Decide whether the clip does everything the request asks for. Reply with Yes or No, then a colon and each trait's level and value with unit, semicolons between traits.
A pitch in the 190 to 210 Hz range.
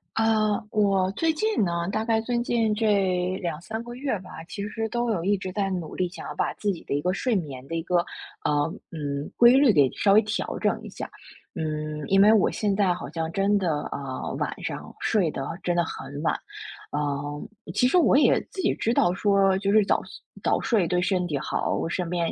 Yes: high, 195 Hz